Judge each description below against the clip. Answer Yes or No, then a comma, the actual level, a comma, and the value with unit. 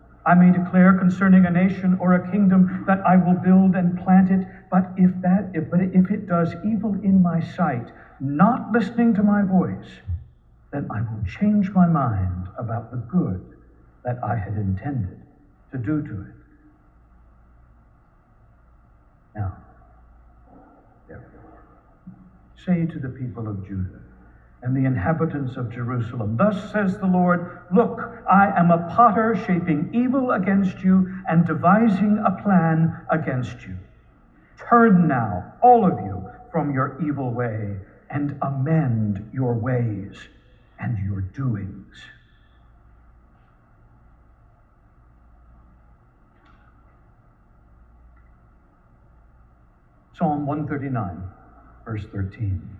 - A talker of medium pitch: Yes, medium, 145 Hz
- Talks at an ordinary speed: No, slow, 115 wpm